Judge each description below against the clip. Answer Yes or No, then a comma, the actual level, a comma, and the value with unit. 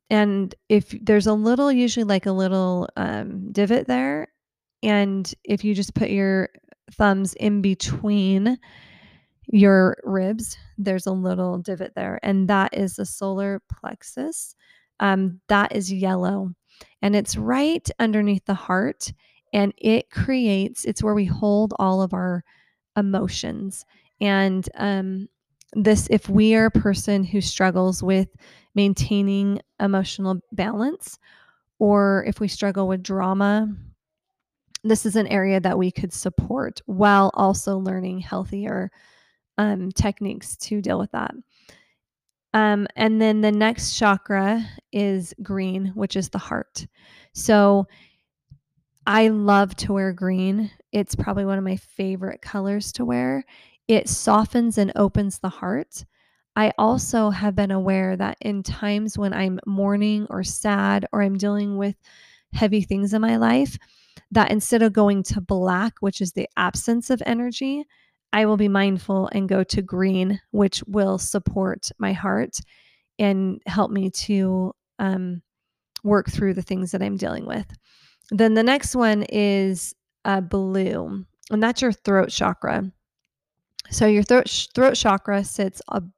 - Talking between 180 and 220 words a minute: No, average, 145 wpm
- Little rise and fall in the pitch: Yes, narrow, 1.8 semitones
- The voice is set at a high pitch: Yes, high, 200 Hz